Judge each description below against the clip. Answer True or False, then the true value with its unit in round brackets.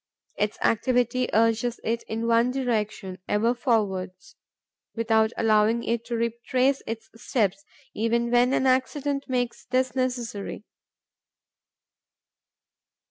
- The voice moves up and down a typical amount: False (2.3 semitones)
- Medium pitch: False (235 Hz)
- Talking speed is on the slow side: True (105 wpm)